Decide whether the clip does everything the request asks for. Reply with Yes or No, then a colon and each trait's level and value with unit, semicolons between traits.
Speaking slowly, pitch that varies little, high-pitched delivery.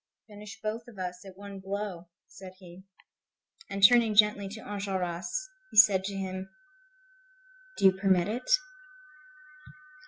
Yes: slow, 130 wpm; narrow, 1.9 semitones; high, 195 Hz